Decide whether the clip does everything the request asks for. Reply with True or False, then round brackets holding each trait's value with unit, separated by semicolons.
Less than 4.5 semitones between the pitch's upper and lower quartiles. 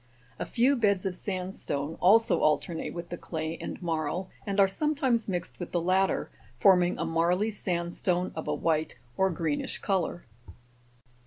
True (2.8 semitones)